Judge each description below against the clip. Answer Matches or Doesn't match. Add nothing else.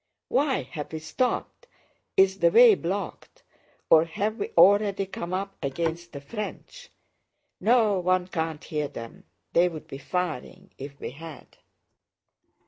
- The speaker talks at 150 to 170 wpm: Doesn't match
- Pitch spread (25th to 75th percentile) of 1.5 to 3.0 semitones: Doesn't match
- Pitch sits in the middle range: Matches